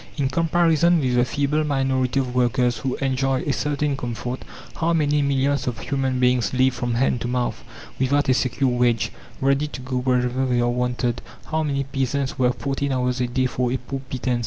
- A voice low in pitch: Yes, low, 130 Hz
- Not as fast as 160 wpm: No, average, 195 wpm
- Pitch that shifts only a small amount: Yes, narrow, 2.0 semitones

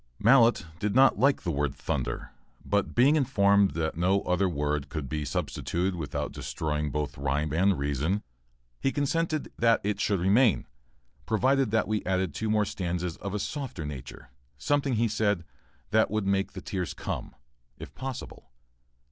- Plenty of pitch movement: Yes, wide, 6.3 semitones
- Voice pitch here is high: No, very low, 95 Hz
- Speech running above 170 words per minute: No, average, 155 wpm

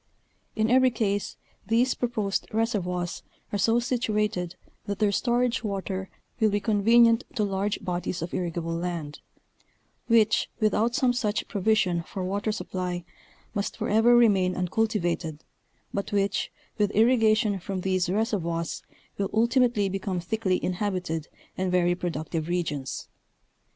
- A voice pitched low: No, high, 200 Hz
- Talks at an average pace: No, slow, 130 wpm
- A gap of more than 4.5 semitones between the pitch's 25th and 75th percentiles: No, average, 3.7 semitones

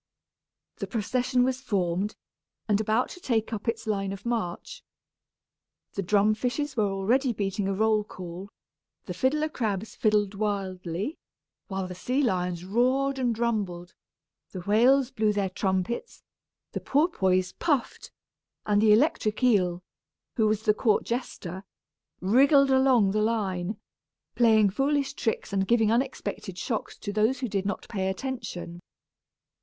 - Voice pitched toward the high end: Yes, high, 215 Hz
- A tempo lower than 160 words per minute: Yes, average, 140 wpm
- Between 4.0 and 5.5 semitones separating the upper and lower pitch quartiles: Yes, average, 4.4 semitones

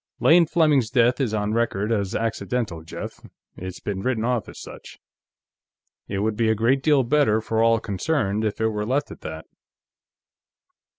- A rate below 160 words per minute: No, average, 170 wpm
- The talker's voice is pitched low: Yes, low, 110 Hz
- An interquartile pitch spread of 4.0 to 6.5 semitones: No, average, 3.5 semitones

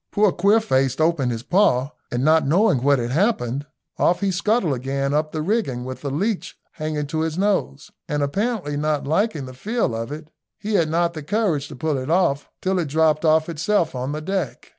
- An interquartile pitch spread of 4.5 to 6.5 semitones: Yes, average, 5.3 semitones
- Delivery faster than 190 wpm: Yes, fast, 205 wpm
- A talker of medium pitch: Yes, medium, 155 Hz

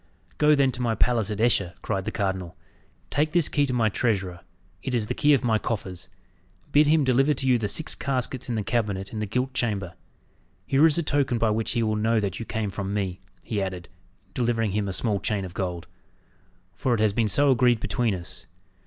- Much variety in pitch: No, average, 4.3 semitones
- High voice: No, low, 110 Hz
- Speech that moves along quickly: Yes, fast, 220 wpm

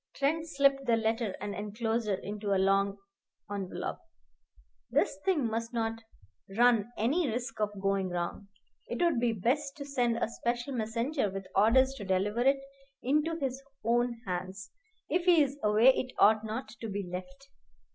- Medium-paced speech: Yes, average, 150 wpm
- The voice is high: Yes, high, 230 Hz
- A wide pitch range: No, average, 4.7 semitones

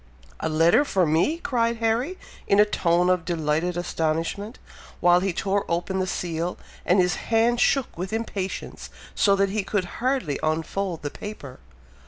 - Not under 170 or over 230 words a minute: No, average, 160 wpm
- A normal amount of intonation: Yes, average, 4.5 semitones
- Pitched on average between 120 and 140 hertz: No, medium, 185 Hz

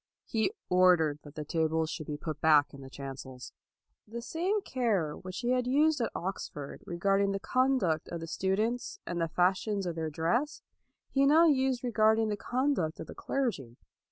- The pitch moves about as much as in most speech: No, wide, 7.8 semitones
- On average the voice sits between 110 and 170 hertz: No, high, 195 Hz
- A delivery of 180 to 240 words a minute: Yes, average, 185 wpm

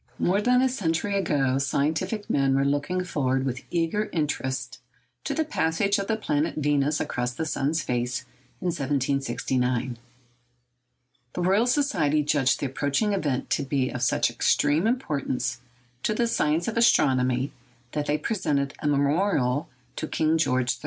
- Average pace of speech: Yes, average, 155 wpm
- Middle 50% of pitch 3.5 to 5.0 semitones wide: No, wide, 5.4 semitones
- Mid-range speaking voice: Yes, medium, 145 Hz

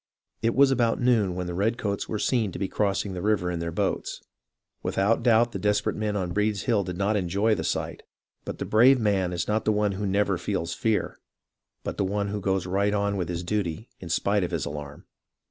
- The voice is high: No, low, 100 Hz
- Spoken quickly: Yes, fast, 220 wpm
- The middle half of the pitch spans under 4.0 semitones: Yes, average, 2.9 semitones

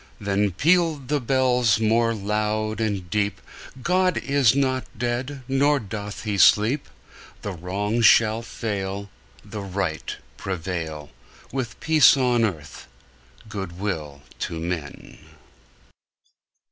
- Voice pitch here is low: Yes, low, 110 Hz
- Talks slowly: Yes, slow, 110 wpm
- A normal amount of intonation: Yes, average, 4.8 semitones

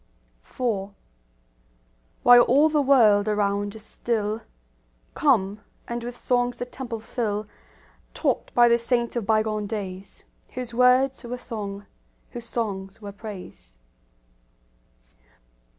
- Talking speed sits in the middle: No, slow, 115 wpm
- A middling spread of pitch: Yes, average, 3.1 semitones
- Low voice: No, high, 225 Hz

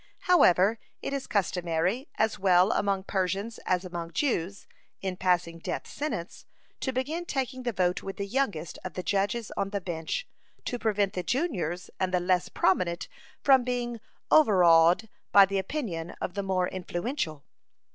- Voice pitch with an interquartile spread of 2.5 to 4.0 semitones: No, average, 4.9 semitones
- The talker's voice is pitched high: Yes, high, 195 Hz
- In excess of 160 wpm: No, average, 155 wpm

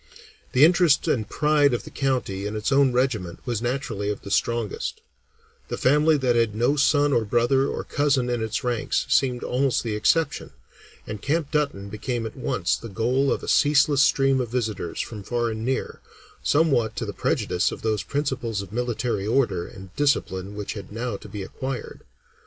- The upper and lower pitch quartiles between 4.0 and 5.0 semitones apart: Yes, average, 4.3 semitones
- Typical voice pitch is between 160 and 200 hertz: No, low, 120 Hz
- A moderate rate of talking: Yes, average, 185 wpm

